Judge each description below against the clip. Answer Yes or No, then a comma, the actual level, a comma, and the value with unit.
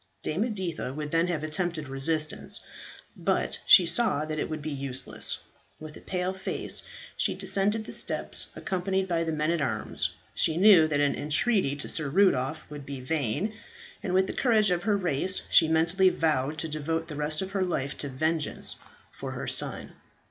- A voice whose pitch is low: No, medium, 160 Hz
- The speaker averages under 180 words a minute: No, average, 185 wpm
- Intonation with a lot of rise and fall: No, average, 4.1 semitones